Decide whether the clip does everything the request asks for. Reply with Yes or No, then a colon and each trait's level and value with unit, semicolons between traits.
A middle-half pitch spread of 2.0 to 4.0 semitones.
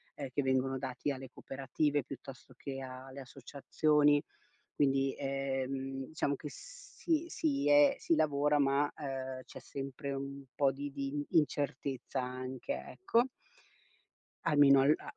No: narrow, 1.6 semitones